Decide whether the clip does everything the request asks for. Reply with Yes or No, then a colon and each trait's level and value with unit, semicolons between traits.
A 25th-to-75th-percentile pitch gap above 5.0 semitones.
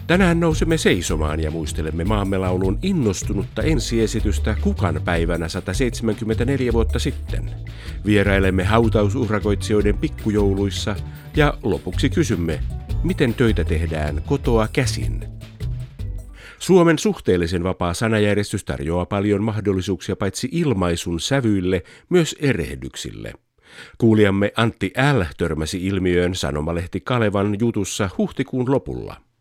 No: average, 4.5 semitones